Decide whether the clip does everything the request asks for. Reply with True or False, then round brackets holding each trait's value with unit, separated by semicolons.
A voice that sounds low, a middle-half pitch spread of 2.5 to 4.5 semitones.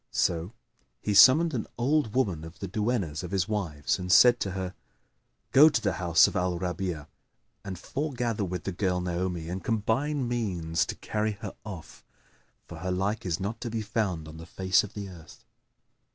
True (95 Hz; 4.0 semitones)